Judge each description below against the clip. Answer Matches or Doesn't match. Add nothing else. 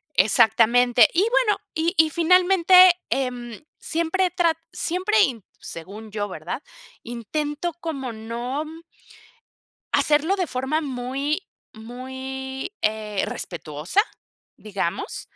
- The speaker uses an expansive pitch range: Matches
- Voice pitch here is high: Matches